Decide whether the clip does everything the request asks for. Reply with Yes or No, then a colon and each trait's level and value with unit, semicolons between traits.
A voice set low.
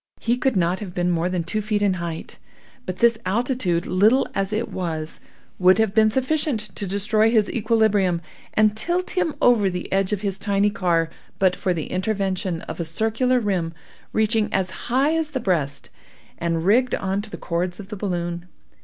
No: high, 200 Hz